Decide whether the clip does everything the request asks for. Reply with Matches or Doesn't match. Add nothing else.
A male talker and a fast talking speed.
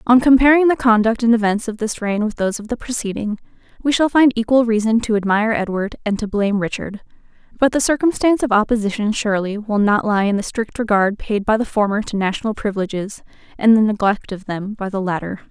Doesn't match